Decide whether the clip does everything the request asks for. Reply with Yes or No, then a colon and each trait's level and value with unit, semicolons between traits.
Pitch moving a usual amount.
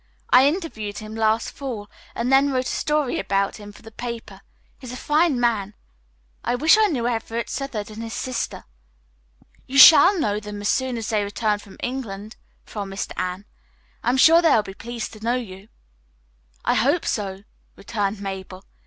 Yes: average, 4.1 semitones